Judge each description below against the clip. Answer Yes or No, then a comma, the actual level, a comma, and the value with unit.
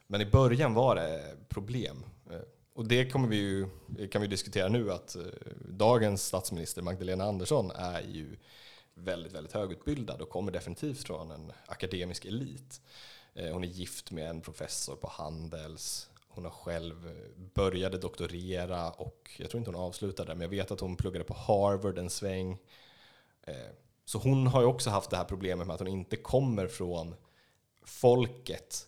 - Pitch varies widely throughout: No, average, 4.6 semitones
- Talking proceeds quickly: No, average, 160 wpm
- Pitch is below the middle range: Yes, very low, 95 Hz